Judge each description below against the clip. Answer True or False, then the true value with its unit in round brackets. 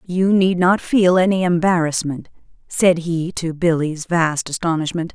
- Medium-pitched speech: True (170 Hz)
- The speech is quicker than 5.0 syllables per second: False (4.3 syllables/s)